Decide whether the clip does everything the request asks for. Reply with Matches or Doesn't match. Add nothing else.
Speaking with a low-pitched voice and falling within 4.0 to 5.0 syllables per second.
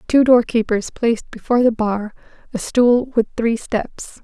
Doesn't match